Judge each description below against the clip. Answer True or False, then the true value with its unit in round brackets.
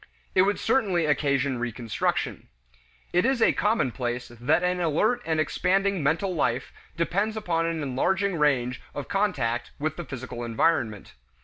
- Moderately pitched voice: True (155 Hz)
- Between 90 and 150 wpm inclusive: True (140 wpm)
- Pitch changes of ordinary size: False (7.0 semitones)